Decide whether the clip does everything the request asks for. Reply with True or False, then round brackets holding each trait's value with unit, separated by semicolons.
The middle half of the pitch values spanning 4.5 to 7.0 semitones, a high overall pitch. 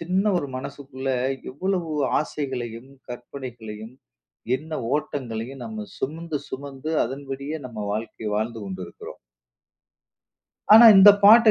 False (5.2 semitones; 135 Hz)